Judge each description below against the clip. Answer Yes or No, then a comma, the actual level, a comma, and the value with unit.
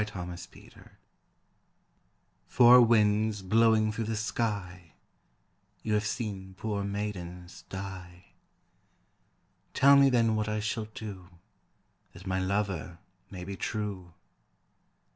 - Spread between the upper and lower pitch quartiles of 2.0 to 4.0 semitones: Yes, average, 2.8 semitones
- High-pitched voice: No, low, 105 Hz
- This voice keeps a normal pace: No, slow, 105 wpm